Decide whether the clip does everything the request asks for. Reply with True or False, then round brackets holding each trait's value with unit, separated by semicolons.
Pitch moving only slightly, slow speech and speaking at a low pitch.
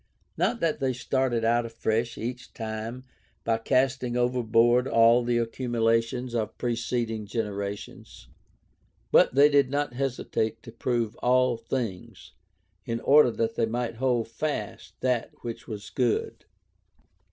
True (1.9 semitones; 130 wpm; 120 Hz)